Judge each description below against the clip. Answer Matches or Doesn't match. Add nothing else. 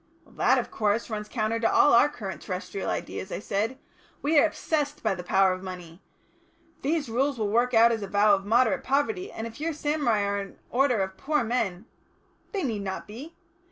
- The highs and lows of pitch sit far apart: Matches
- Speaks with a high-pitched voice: Matches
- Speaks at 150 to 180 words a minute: Doesn't match